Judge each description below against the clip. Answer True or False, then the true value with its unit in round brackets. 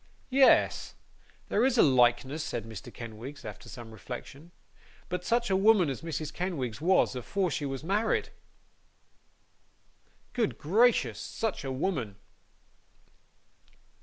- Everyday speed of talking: False (120 wpm)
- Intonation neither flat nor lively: False (7.8 semitones)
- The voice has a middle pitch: True (150 Hz)